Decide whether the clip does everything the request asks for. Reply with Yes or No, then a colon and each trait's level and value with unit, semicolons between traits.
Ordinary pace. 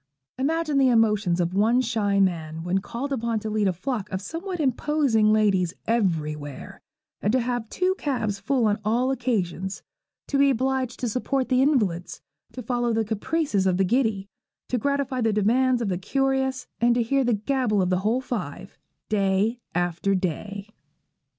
Yes: average, 170 wpm